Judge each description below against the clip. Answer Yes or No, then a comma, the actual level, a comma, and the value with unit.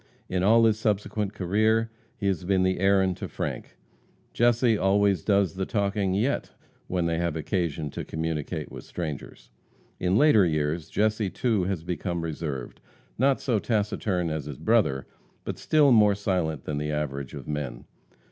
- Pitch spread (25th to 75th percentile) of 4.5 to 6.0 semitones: Yes, average, 4.8 semitones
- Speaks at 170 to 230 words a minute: No, average, 160 wpm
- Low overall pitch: Yes, very low, 95 Hz